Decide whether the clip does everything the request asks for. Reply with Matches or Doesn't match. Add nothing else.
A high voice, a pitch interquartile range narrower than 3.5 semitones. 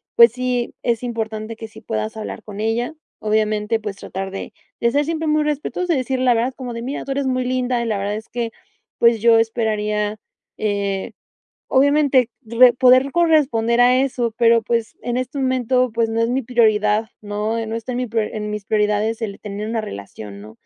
Matches